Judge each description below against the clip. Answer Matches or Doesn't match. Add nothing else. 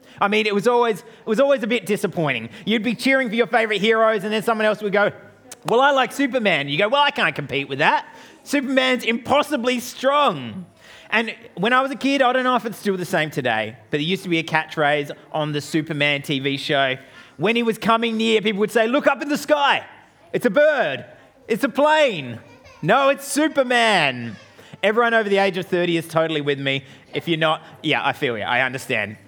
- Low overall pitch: Doesn't match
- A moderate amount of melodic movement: Doesn't match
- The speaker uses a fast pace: Matches